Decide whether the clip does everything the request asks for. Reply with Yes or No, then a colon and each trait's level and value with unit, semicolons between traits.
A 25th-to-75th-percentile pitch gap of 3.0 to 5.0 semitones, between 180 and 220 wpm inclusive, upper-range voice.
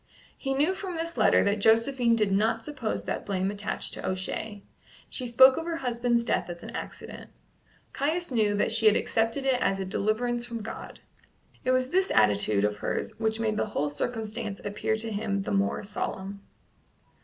Yes: average, 3.8 semitones; average, 185 wpm; high, 225 Hz